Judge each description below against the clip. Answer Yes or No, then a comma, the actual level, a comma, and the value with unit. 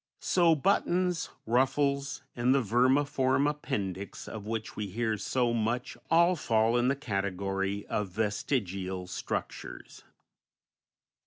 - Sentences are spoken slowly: Yes, slow, 110 wpm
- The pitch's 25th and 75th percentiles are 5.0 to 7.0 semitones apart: Yes, wide, 5.4 semitones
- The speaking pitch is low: Yes, low, 120 Hz